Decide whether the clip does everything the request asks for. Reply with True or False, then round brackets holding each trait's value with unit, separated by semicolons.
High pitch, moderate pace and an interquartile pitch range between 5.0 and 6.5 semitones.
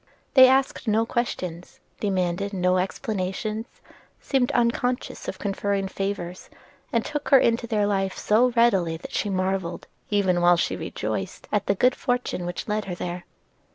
False (200 Hz; 155 wpm; 4.2 semitones)